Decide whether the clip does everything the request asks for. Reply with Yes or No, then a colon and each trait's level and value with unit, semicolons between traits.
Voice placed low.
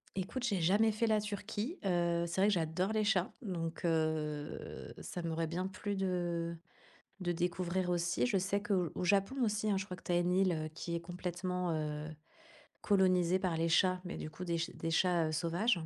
No: medium, 180 Hz